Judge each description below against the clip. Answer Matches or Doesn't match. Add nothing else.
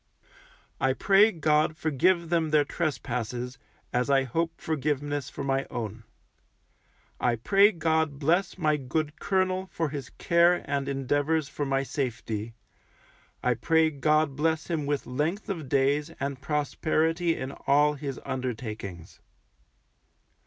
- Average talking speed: Doesn't match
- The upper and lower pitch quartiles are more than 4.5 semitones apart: Doesn't match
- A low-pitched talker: Doesn't match